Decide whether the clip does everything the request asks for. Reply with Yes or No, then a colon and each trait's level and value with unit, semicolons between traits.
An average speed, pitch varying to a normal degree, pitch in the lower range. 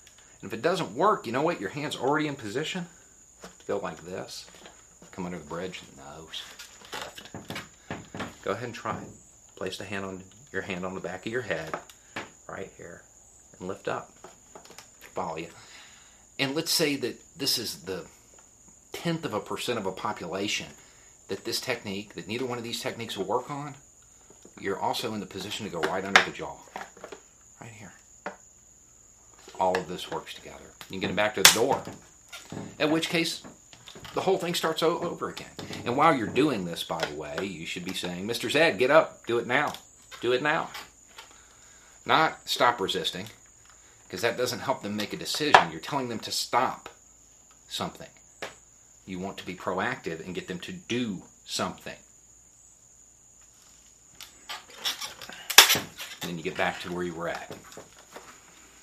No: average, 170 wpm; wide, 7.4 semitones; low, 115 Hz